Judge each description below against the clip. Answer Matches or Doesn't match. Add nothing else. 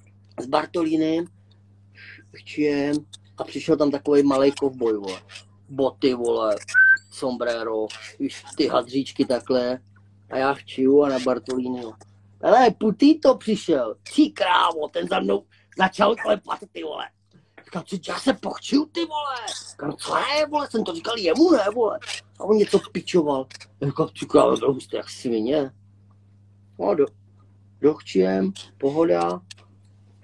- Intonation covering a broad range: Matches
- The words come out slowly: Doesn't match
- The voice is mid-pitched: Doesn't match